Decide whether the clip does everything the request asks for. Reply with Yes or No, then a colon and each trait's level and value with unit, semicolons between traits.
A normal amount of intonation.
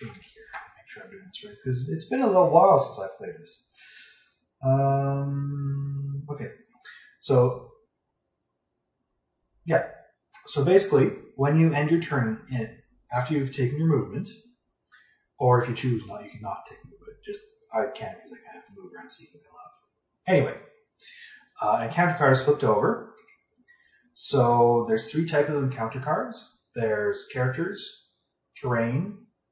No: wide, 6.1 semitones